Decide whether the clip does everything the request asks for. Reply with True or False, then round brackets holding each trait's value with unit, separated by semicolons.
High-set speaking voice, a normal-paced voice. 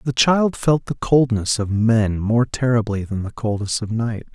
False (115 Hz; 195 wpm)